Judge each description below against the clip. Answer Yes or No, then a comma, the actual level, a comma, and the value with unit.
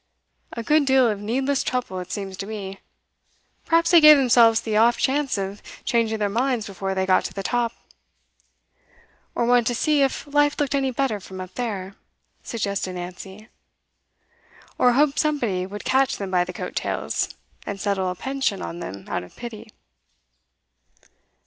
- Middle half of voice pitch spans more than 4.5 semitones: Yes, wide, 5.4 semitones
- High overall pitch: Yes, high, 225 Hz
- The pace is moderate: Yes, average, 170 wpm